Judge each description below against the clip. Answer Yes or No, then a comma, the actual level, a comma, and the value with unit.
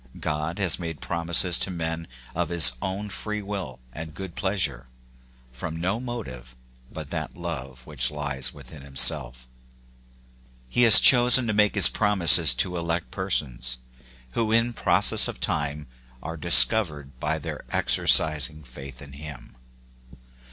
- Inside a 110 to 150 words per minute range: Yes, slow, 135 wpm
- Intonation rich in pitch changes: Yes, wide, 5.7 semitones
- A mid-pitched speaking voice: No, very low, 80 Hz